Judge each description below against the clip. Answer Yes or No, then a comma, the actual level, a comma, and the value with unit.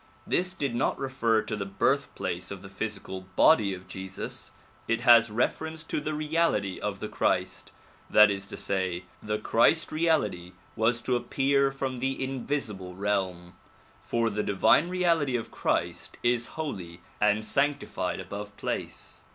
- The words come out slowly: No, average, 150 wpm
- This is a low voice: Yes, low, 115 Hz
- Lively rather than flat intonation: Yes, wide, 6.0 semitones